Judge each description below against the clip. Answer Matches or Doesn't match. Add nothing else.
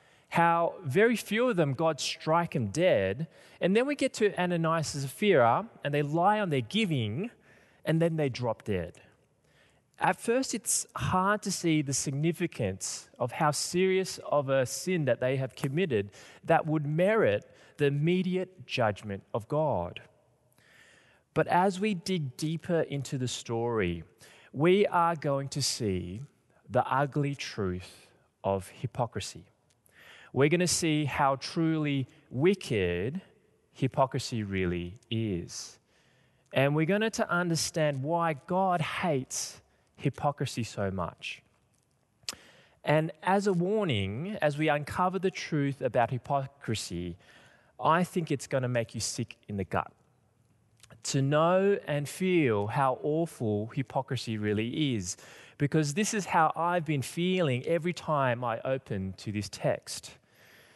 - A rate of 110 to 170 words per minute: Matches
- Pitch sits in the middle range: Matches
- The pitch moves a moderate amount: Doesn't match